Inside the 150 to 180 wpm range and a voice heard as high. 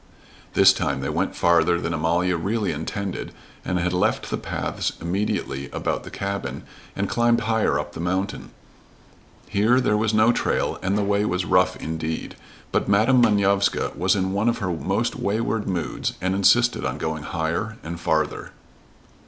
No: average, 165 wpm; very low, 95 Hz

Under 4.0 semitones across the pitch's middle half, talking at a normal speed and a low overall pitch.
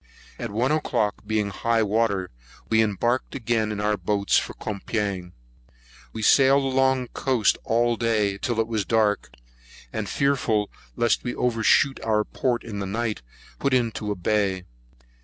Yes: narrow, 2.6 semitones; average, 160 wpm; low, 110 Hz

